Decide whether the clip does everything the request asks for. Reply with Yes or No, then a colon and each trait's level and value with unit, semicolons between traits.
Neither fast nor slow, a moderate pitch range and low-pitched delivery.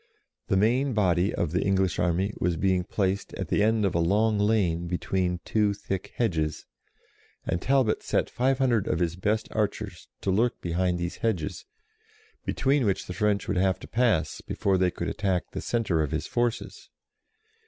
Yes: average, 175 wpm; average, 3.7 semitones; very low, 95 Hz